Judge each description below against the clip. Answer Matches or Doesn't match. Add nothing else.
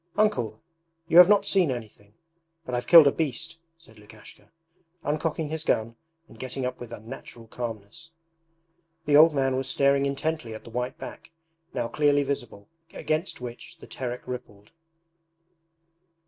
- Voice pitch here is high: Doesn't match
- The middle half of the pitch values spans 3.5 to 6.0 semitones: Matches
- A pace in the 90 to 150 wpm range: Matches